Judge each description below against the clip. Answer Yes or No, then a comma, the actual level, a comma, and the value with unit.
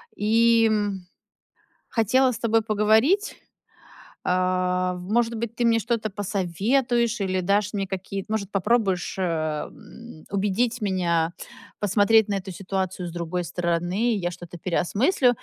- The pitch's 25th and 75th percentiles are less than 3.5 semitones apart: No, average, 3.8 semitones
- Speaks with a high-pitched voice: Yes, high, 200 Hz